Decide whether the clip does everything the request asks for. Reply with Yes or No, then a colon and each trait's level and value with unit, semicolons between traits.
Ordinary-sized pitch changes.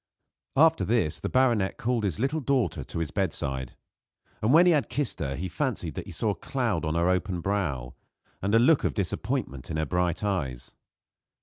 No: wide, 7.7 semitones